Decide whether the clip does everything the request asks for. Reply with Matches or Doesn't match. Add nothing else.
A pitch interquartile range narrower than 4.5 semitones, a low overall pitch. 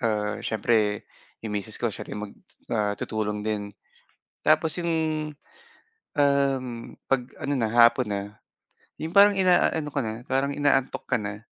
Doesn't match